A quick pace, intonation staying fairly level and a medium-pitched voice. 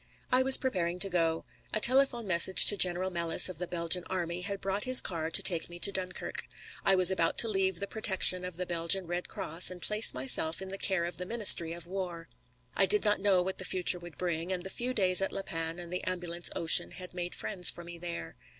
Yes: fast, 235 wpm; narrow, 2.1 semitones; medium, 180 Hz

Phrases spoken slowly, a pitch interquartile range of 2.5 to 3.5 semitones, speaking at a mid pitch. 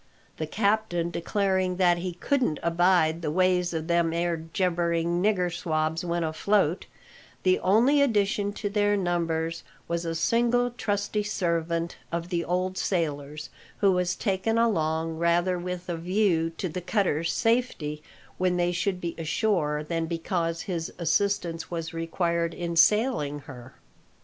No: average, 145 wpm; average, 3.0 semitones; medium, 175 Hz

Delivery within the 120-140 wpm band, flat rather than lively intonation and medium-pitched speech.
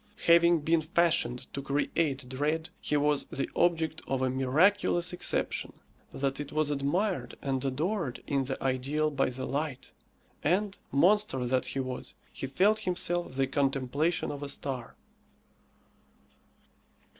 No: slow, 135 wpm; average, 4.0 semitones; medium, 145 Hz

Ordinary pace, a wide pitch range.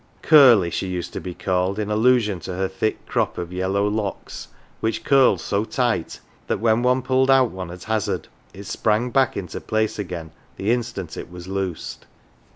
No: average, 180 wpm; average, 4.3 semitones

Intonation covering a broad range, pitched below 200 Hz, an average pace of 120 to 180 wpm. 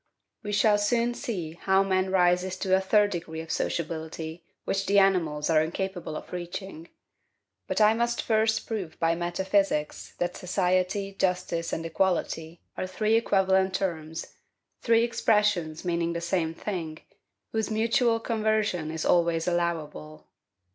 No: average, 3.7 semitones; medium, 185 Hz; average, 140 wpm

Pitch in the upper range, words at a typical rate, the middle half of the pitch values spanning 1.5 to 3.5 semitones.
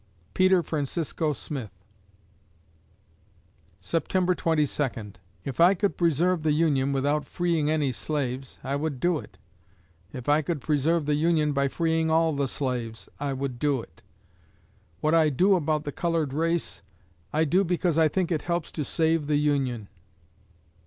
No: medium, 150 Hz; average, 150 wpm; average, 3.1 semitones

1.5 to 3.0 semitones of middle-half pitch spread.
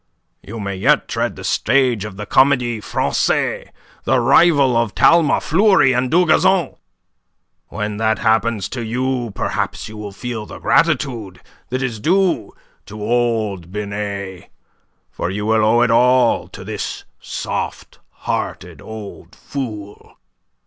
No: average, 3.6 semitones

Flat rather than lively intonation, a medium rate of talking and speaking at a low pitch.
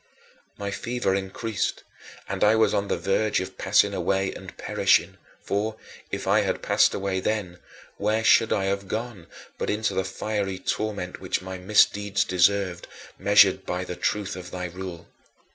Yes: narrow, 2.1 semitones; average, 160 wpm; low, 100 Hz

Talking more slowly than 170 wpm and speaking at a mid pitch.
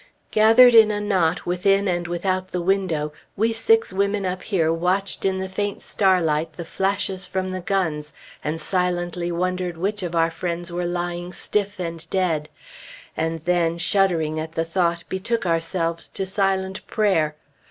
Yes: average, 160 wpm; medium, 180 Hz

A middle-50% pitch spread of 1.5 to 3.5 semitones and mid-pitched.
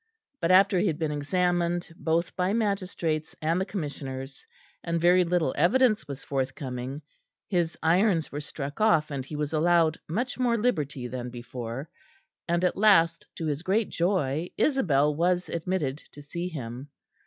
No: average, 4.1 semitones; medium, 165 Hz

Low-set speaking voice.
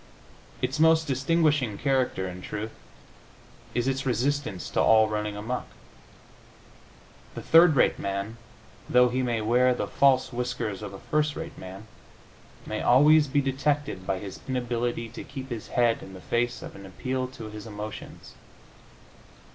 Yes: low, 125 Hz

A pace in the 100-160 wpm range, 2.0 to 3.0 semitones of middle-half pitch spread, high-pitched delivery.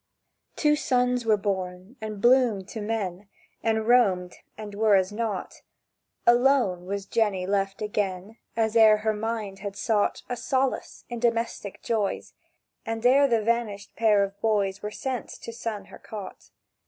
Yes: average, 155 wpm; narrow, 2.6 semitones; high, 215 Hz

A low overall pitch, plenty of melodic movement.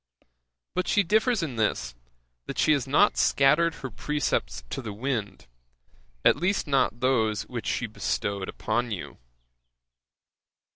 Yes: low, 130 Hz; wide, 6.4 semitones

